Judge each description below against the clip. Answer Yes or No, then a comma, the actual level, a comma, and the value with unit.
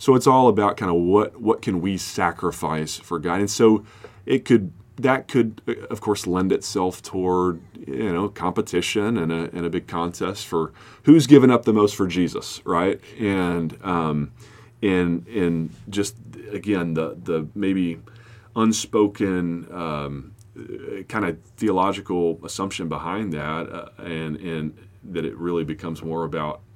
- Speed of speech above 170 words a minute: No, average, 155 wpm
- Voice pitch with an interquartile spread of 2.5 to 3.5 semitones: No, average, 4.4 semitones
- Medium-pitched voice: No, very low, 90 Hz